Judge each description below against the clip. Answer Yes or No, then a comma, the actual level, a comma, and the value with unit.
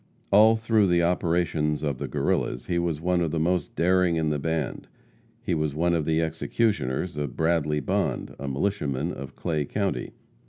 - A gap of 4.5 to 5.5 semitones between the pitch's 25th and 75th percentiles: No, average, 3.2 semitones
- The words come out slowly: No, average, 175 wpm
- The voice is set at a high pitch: No, very low, 80 Hz